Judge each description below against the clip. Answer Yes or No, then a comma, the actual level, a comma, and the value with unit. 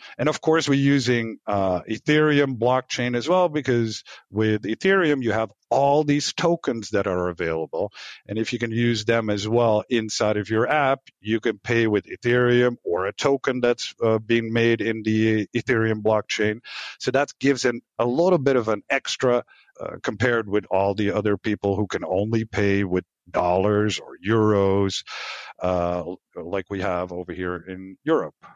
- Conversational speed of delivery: Yes, average, 170 wpm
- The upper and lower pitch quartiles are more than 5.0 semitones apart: No, average, 3.3 semitones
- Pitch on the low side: Yes, low, 110 Hz